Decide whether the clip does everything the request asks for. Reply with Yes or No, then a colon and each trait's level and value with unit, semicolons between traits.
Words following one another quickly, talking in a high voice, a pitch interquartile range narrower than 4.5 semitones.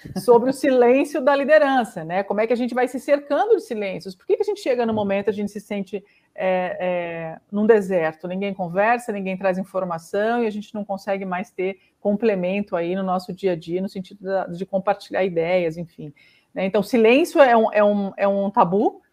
Yes: fast, 215 wpm; high, 200 Hz; average, 4.1 semitones